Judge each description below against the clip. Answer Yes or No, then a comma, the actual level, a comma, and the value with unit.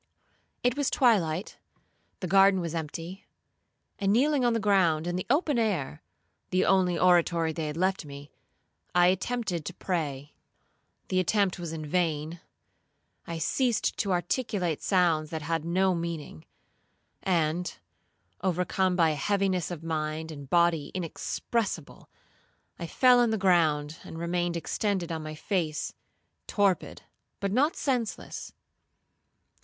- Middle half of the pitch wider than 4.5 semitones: No, average, 3.5 semitones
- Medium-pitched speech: Yes, medium, 175 Hz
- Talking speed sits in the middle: No, slow, 130 wpm